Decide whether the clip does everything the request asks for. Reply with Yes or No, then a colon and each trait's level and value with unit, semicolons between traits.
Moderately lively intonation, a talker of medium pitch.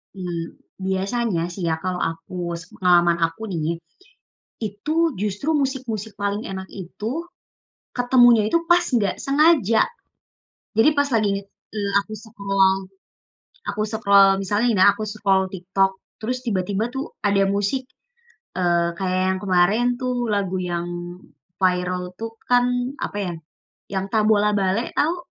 No: average, 3.3 semitones; high, 200 Hz